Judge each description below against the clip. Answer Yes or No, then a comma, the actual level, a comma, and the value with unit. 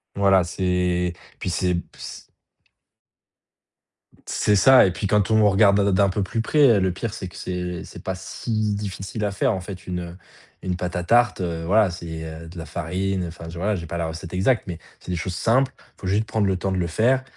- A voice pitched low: Yes, very low, 95 Hz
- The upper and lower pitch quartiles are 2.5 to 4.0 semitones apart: Yes, average, 2.9 semitones